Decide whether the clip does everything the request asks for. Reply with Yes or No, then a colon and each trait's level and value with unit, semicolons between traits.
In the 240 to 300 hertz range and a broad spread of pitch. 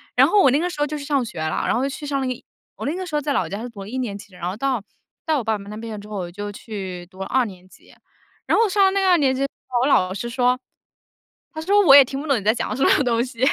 Yes: very high, 250 Hz; wide, 6.0 semitones